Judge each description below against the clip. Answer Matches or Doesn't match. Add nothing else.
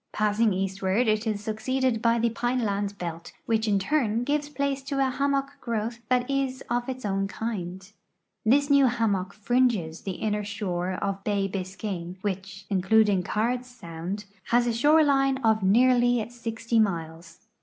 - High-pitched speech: Matches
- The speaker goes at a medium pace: Matches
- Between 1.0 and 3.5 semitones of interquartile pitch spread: Doesn't match